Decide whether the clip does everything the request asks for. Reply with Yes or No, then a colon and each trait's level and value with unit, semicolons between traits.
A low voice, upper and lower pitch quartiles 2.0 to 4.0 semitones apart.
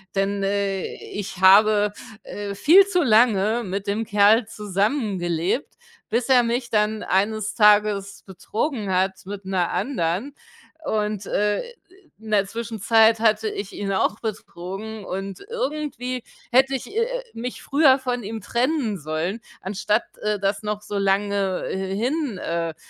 No: high, 210 Hz; average, 3.0 semitones